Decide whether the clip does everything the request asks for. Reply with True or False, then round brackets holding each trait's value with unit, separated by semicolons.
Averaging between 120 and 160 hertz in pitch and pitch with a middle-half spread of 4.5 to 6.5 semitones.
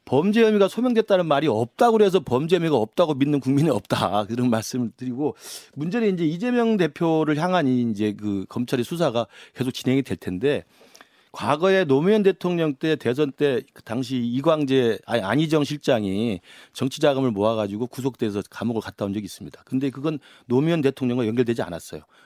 True (135 Hz; 5.6 semitones)